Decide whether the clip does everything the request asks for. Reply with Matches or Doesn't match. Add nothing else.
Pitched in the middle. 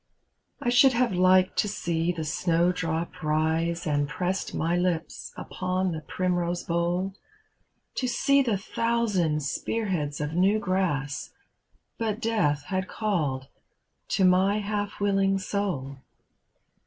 Matches